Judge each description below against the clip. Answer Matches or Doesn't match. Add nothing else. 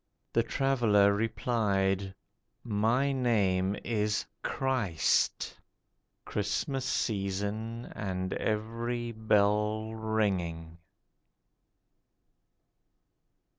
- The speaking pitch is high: Doesn't match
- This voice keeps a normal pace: Doesn't match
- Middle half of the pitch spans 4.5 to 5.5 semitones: Doesn't match